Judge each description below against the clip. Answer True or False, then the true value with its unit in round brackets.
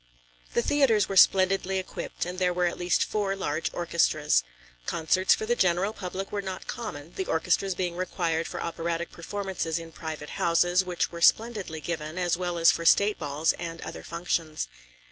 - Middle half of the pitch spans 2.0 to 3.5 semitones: True (2.5 semitones)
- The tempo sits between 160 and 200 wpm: True (175 wpm)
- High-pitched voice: False (175 Hz)